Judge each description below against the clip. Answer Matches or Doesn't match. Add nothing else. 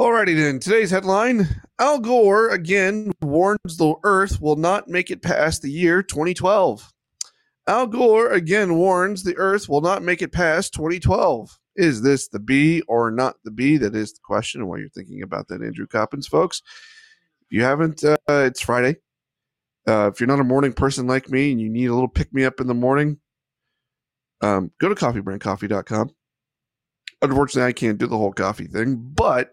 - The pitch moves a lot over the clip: Matches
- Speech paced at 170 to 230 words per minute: Matches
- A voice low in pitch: Doesn't match